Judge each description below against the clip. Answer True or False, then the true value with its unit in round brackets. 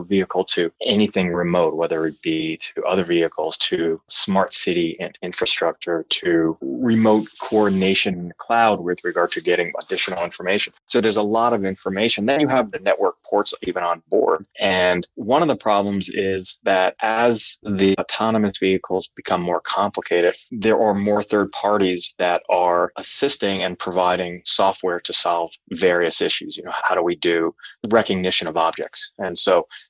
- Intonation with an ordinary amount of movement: True (3.0 semitones)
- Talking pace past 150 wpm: True (165 wpm)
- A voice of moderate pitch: False (95 Hz)